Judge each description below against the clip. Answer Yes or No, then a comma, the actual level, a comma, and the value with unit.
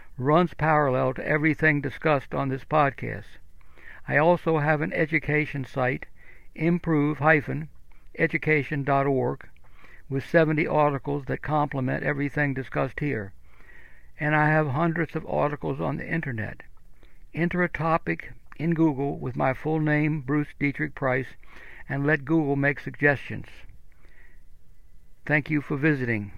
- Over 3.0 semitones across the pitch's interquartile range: No, narrow, 2.5 semitones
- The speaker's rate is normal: No, slow, 120 wpm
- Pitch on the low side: No, medium, 150 Hz